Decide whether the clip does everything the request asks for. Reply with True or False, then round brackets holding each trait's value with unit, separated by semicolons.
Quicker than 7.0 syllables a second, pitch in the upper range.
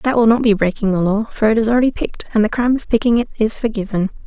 True (7.2 syllables/s; 220 Hz)